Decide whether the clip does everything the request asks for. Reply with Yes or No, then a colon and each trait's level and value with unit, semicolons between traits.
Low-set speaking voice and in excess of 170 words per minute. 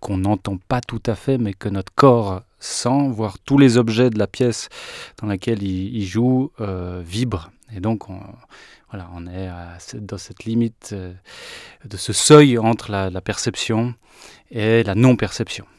No: low, 110 Hz; average, 165 wpm